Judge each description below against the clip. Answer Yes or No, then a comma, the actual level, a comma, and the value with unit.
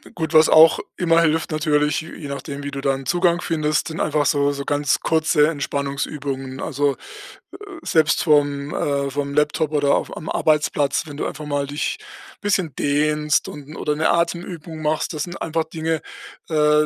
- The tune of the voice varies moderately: No, narrow, 1.9 semitones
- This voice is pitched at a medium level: Yes, medium, 150 Hz